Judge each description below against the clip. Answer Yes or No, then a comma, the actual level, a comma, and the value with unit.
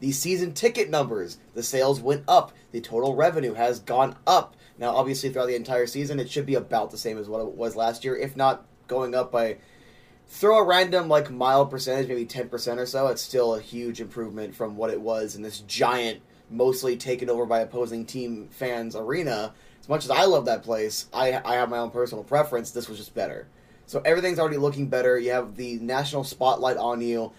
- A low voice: Yes, low, 125 Hz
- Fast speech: Yes, fast, 215 wpm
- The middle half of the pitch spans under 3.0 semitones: Yes, narrow, 2.5 semitones